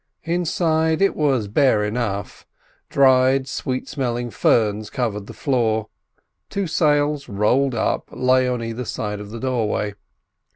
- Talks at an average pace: No, slow, 130 wpm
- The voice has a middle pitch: No, low, 125 Hz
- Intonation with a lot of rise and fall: No, average, 4.3 semitones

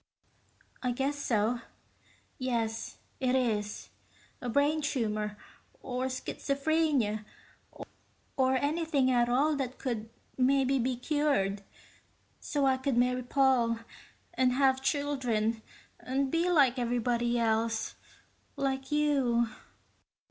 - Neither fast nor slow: No, slow, 105 wpm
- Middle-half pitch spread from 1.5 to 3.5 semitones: Yes, average, 2.9 semitones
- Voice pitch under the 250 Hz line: No, very high, 255 Hz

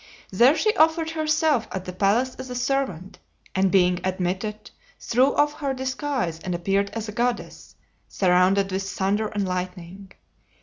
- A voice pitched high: Yes, high, 205 Hz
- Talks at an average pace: Yes, average, 150 wpm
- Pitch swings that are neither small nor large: No, wide, 5.9 semitones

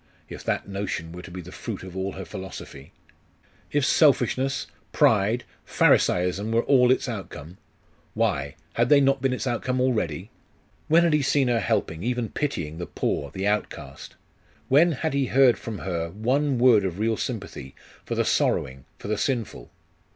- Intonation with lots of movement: Yes, wide, 6.4 semitones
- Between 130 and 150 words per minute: No, average, 170 wpm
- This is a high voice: No, low, 110 Hz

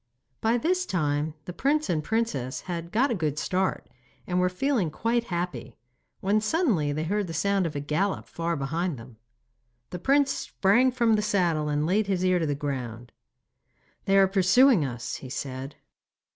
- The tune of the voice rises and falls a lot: Yes, wide, 6.2 semitones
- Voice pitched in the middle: Yes, medium, 180 Hz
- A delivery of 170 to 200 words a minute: Yes, average, 175 wpm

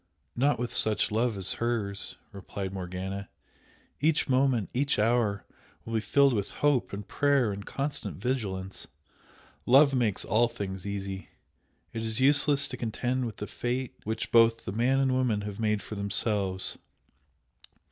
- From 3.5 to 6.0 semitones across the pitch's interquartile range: Yes, average, 4.3 semitones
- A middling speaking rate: Yes, average, 150 wpm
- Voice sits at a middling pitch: No, low, 115 Hz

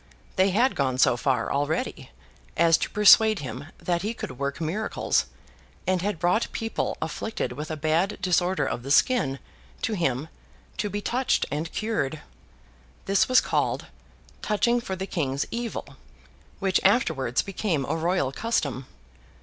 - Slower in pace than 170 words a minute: Yes, average, 150 wpm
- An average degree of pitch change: No, wide, 6.7 semitones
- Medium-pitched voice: Yes, medium, 175 Hz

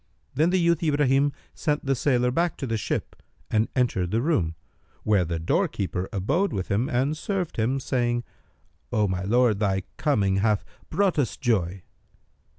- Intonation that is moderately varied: No, wide, 6.8 semitones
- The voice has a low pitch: Yes, low, 120 Hz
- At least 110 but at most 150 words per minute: No, average, 160 wpm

